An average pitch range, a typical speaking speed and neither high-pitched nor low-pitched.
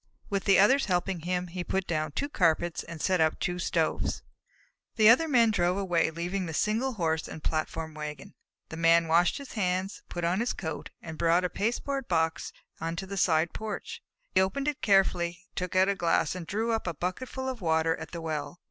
No: average, 3.7 semitones; fast, 210 wpm; medium, 180 Hz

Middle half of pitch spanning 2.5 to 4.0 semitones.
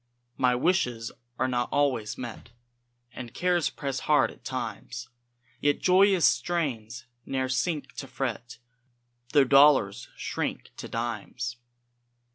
Yes: average, 3.4 semitones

